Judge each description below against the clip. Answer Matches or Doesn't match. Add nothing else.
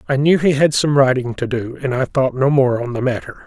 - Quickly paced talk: Matches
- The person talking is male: Matches